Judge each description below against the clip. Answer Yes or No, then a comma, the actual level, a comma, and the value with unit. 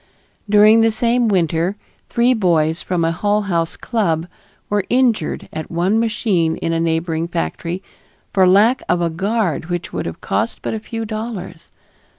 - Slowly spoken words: No, average, 165 wpm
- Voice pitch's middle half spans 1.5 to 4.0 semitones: No, average, 4.8 semitones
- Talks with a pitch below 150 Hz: No, high, 190 Hz